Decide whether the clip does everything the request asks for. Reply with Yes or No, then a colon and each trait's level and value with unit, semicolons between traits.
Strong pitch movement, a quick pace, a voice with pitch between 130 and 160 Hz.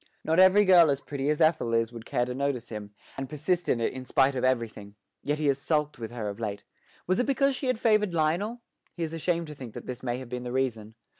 Yes: wide, 5.9 semitones; fast, 255 wpm; medium, 140 Hz